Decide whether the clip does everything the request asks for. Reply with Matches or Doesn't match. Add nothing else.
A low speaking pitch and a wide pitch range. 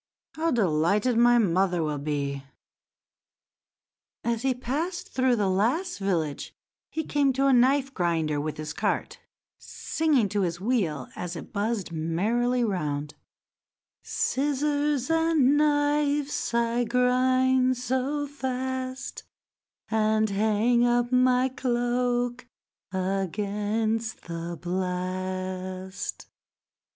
Doesn't match